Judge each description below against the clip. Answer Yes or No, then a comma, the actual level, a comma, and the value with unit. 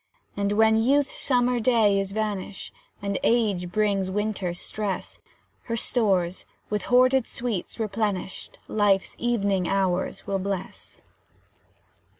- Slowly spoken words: Yes, slow, 115 wpm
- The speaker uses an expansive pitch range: No, average, 2.9 semitones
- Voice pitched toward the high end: Yes, high, 205 Hz